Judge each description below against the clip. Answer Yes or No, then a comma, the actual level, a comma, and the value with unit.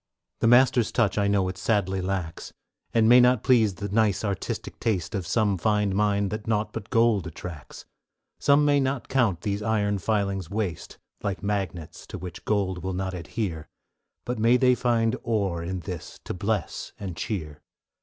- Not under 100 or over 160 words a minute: No, average, 170 wpm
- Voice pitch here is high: No, low, 100 Hz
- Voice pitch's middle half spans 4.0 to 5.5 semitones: No, average, 3.3 semitones